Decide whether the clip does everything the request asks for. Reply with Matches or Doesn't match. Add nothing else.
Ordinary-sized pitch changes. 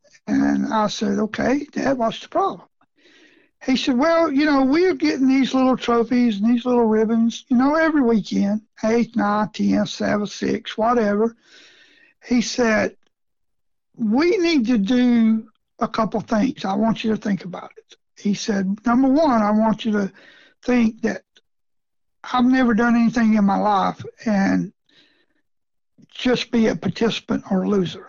Matches